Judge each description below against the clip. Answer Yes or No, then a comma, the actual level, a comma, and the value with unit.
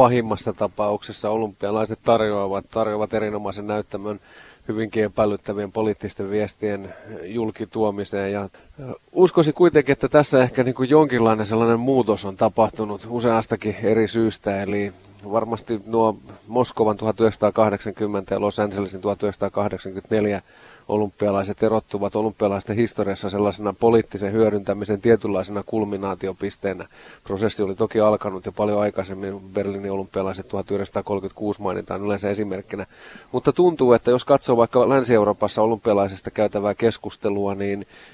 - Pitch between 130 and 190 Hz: No, low, 105 Hz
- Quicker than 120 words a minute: No, average, 110 wpm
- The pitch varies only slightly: Yes, narrow, 2.0 semitones